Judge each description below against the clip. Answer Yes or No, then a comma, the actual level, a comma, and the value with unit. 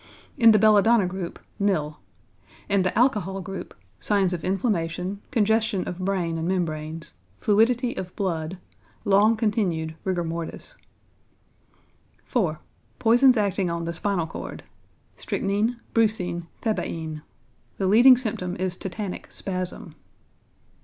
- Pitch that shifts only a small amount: No, average, 3.9 semitones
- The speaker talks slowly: Yes, slow, 115 wpm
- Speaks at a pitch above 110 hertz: Yes, high, 190 Hz